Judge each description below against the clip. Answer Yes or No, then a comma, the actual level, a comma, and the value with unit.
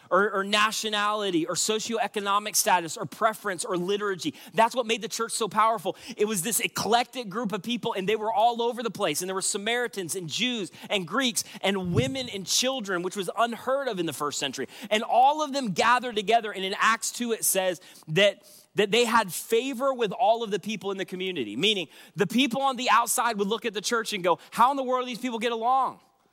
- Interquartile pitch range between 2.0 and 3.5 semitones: Yes, average, 3.2 semitones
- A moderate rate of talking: No, fast, 225 wpm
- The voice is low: No, high, 220 Hz